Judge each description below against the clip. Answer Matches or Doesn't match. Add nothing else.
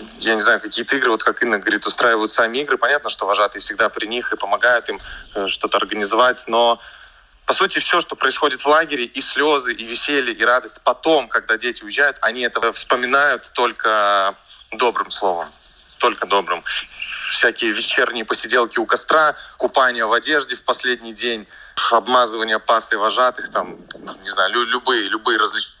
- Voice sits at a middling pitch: Doesn't match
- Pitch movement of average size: Doesn't match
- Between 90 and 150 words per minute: Doesn't match